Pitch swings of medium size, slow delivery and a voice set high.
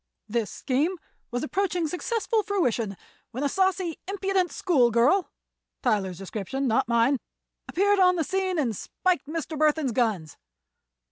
No: wide, 8.0 semitones; slow, 120 wpm; very high, 300 Hz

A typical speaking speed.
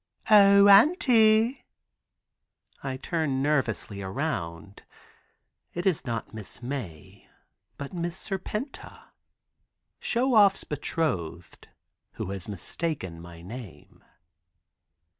No: slow, 85 wpm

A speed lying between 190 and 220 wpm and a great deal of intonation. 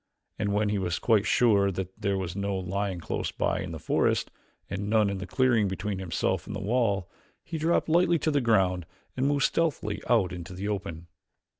No: average, 200 wpm; average, 3.6 semitones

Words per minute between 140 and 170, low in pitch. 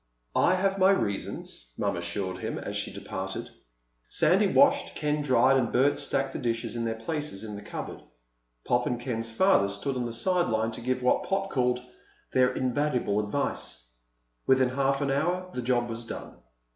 No: average, 180 wpm; low, 125 Hz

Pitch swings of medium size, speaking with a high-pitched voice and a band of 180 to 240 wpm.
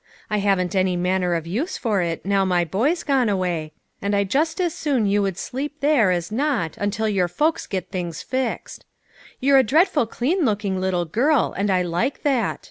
No: wide, 6.8 semitones; high, 205 Hz; average, 195 wpm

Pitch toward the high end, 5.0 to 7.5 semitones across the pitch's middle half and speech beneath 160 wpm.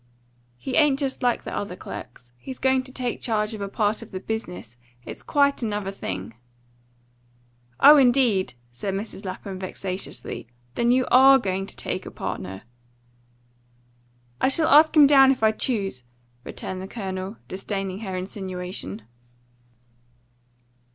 Yes: high, 205 Hz; wide, 5.5 semitones; average, 145 wpm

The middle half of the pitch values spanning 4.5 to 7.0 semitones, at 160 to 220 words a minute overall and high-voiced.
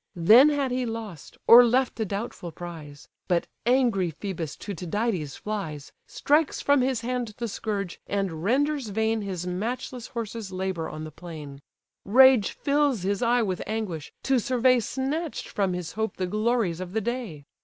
Yes: wide, 5.6 semitones; average, 165 wpm; high, 215 Hz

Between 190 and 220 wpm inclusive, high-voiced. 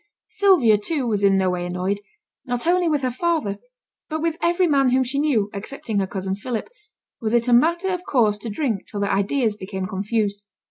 Yes: average, 200 wpm; high, 235 Hz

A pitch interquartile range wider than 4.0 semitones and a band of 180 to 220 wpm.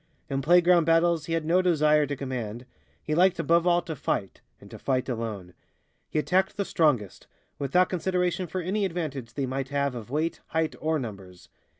Yes: average, 4.9 semitones; average, 185 wpm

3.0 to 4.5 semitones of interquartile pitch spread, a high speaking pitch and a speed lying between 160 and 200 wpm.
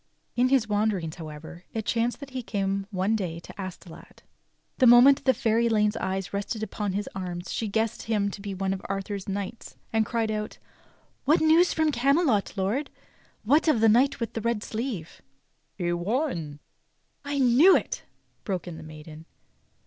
Yes: average, 4.1 semitones; high, 210 Hz; average, 180 wpm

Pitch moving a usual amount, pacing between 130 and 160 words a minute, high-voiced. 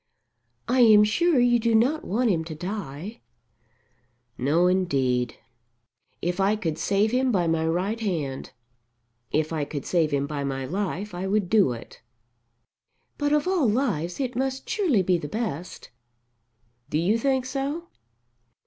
No: wide, 7.1 semitones; average, 150 wpm; high, 195 Hz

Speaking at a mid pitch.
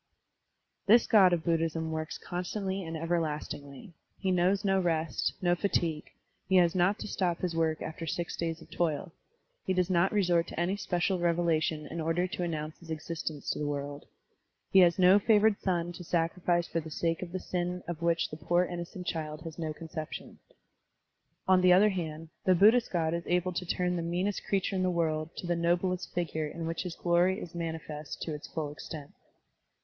Yes: medium, 170 Hz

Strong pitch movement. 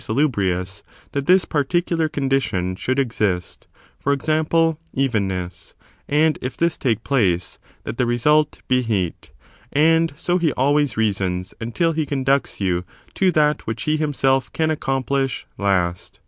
Yes: wide, 6.9 semitones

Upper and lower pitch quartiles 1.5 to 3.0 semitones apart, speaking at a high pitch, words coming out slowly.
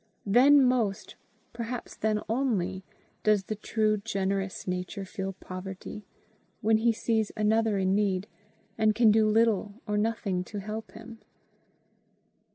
Yes: narrow, 2.4 semitones; high, 215 Hz; slow, 130 wpm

